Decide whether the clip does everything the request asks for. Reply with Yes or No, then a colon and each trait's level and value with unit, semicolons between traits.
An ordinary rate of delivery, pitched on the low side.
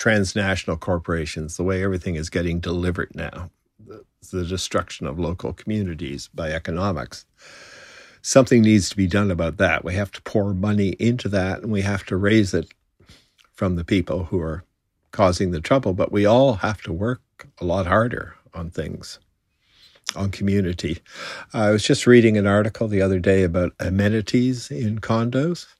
Yes: average, 165 wpm; very low, 95 Hz